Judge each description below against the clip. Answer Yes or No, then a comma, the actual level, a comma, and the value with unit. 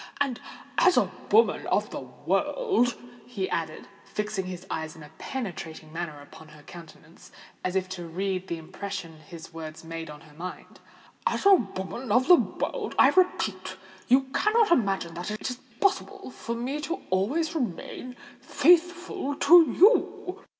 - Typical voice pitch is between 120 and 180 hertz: No, high, 200 Hz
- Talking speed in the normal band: Yes, average, 155 wpm